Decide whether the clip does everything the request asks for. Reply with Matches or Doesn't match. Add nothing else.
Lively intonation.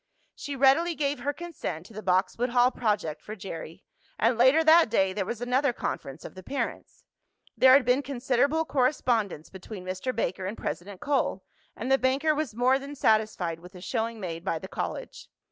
Matches